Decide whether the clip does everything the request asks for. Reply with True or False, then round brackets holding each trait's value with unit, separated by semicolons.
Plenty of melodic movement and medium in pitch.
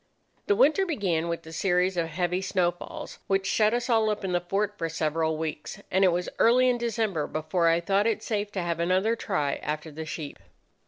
False (4.3 semitones; 180 Hz)